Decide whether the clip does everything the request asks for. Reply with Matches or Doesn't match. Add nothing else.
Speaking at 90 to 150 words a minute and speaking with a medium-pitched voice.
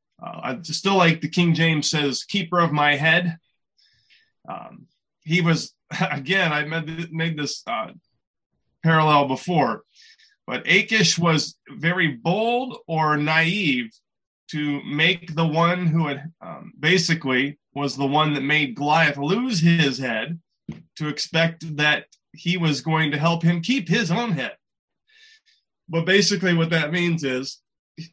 Matches